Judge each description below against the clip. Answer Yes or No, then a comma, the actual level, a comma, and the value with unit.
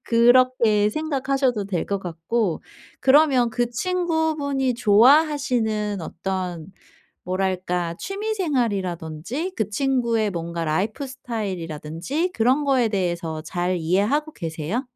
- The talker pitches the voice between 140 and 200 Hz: No, high, 220 Hz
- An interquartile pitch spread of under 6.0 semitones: No, wide, 7.1 semitones